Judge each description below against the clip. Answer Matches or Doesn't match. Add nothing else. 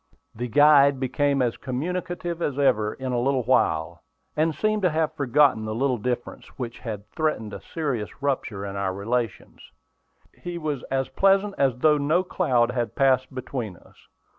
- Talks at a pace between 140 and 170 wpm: Matches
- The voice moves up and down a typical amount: Matches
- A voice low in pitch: Matches